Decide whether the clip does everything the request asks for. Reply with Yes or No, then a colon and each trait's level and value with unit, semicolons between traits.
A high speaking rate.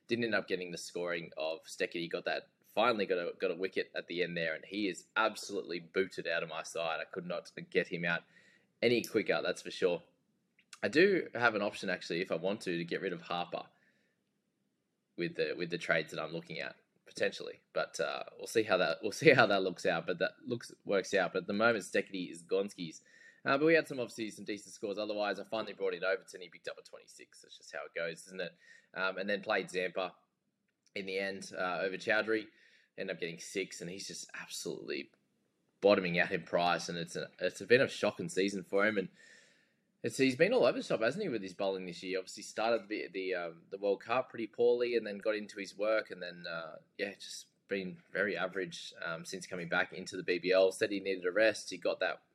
Yes: fast, 235 wpm